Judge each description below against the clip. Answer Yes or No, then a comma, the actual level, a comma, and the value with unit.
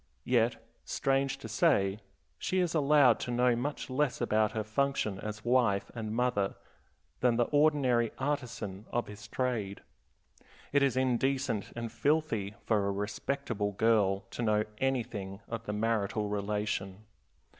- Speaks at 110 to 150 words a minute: Yes, average, 140 wpm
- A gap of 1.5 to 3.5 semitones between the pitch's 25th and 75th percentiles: No, average, 4.1 semitones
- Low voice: Yes, low, 115 Hz